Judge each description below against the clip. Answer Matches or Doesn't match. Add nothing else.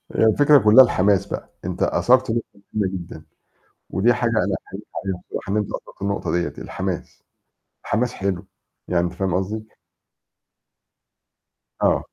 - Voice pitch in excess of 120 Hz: Doesn't match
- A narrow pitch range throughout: Doesn't match